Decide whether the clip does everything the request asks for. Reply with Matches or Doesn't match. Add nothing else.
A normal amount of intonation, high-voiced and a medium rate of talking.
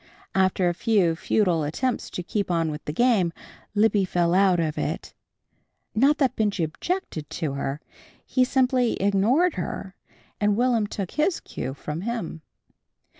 Doesn't match